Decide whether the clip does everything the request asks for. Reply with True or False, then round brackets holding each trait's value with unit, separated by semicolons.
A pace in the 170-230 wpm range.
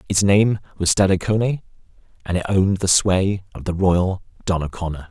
False (155 wpm)